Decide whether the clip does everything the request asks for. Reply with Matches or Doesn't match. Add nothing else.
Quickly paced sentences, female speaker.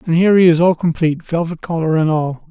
Doesn't match